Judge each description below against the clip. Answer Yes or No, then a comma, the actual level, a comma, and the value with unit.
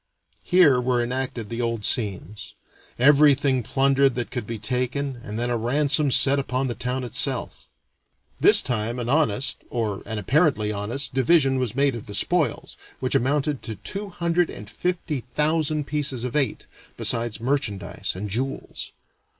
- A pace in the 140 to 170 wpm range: Yes, average, 155 wpm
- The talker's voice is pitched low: Yes, low, 130 Hz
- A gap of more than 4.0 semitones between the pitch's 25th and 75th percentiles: No, average, 3.7 semitones